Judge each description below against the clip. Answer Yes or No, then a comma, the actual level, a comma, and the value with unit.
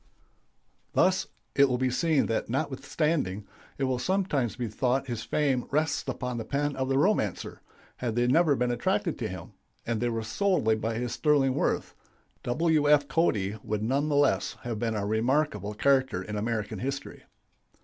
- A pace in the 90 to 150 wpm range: No, average, 175 wpm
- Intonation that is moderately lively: Yes, average, 4.3 semitones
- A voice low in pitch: Yes, low, 130 Hz